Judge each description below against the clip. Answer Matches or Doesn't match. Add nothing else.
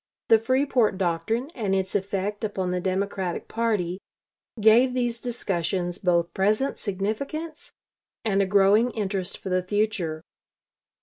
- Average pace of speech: Doesn't match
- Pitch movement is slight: Doesn't match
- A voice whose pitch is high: Matches